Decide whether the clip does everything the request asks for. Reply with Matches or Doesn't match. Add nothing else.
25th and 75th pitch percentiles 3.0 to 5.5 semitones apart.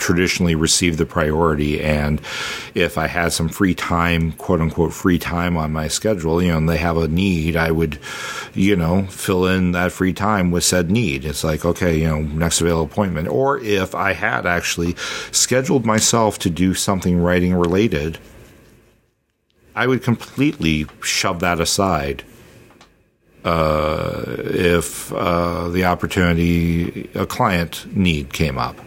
Doesn't match